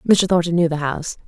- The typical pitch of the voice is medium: Yes, medium, 170 Hz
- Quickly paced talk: Yes, fast, 235 wpm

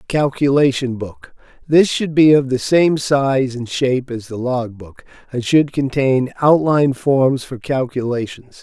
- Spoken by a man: Yes, male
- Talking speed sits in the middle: Yes, average, 145 wpm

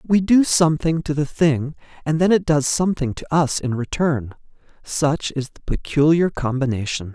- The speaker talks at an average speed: Yes, average, 170 wpm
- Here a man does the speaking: Yes, male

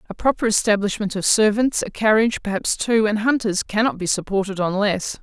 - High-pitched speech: Yes, high, 210 Hz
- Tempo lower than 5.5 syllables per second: No, 5.6 syllables/s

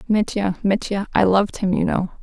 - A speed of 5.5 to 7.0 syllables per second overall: No, 5.3 syllables/s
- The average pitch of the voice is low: No, high, 195 Hz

